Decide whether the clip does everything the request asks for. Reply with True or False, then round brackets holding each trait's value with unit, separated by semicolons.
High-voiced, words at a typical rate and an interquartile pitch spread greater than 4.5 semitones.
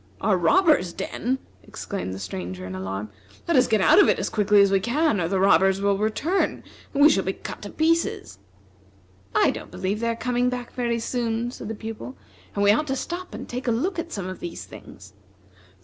False (220 Hz; 215 wpm; 5.1 semitones)